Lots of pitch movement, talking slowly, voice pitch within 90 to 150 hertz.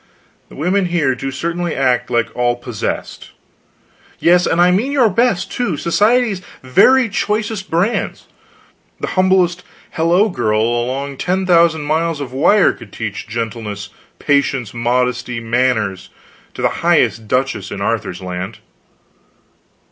Yes: wide, 7.3 semitones; slow, 130 wpm; medium, 140 Hz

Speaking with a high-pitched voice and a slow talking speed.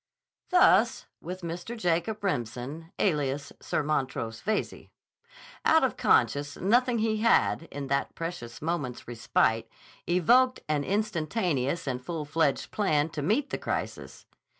No: medium, 165 Hz; slow, 125 wpm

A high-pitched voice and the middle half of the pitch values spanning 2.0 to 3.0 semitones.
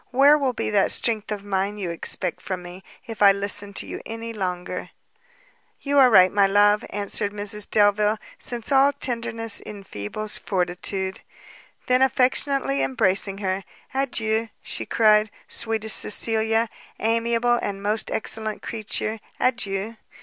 Yes: high, 210 Hz; narrow, 2.6 semitones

